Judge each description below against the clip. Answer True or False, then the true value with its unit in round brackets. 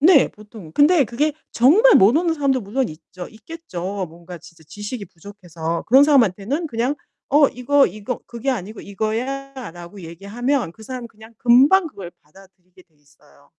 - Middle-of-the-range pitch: False (220 Hz)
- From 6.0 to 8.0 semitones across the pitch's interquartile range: True (7.1 semitones)